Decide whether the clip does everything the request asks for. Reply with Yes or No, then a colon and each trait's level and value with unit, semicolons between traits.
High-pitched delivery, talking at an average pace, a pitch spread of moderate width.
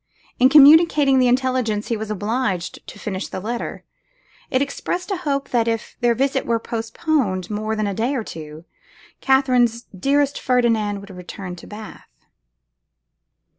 Yes: high, 235 Hz; average, 155 wpm; average, 4.4 semitones